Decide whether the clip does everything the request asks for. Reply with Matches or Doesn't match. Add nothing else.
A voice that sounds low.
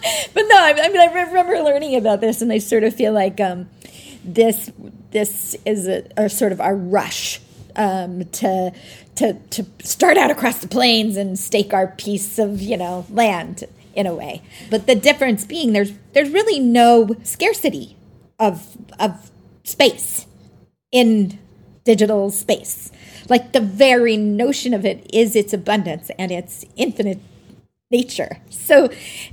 Doesn't match